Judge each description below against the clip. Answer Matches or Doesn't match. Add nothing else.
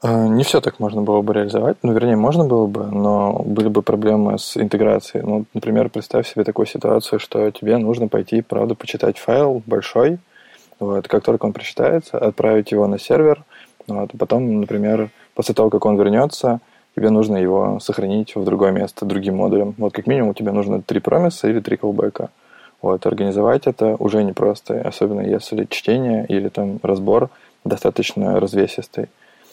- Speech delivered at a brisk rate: Matches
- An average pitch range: Doesn't match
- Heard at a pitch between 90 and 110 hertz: Matches